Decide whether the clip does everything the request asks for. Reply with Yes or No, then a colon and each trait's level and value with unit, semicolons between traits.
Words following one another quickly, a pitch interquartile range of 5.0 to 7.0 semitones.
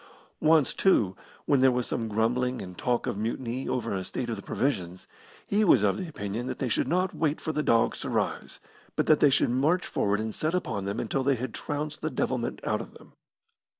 Yes: fast, 220 wpm; average, 5.3 semitones